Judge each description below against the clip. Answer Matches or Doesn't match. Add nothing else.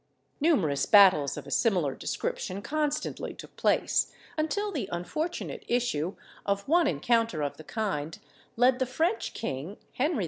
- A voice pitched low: Doesn't match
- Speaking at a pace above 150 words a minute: Doesn't match